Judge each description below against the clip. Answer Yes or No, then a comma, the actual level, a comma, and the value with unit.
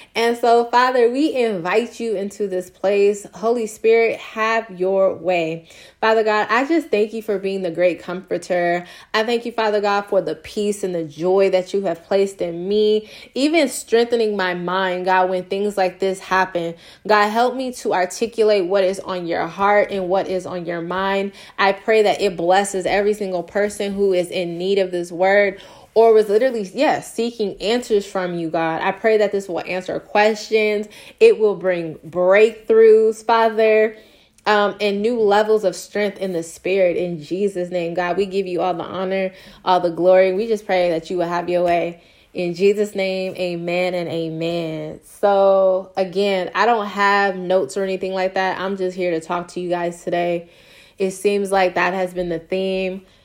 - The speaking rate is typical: Yes, average, 190 wpm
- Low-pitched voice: No, high, 195 Hz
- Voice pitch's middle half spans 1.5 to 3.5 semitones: Yes, average, 2.8 semitones